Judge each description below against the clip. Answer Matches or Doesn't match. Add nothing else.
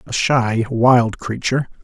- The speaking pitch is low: Matches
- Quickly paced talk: Doesn't match